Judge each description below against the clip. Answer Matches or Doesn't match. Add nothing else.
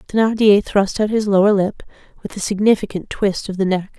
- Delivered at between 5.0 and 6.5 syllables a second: Matches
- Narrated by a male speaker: Doesn't match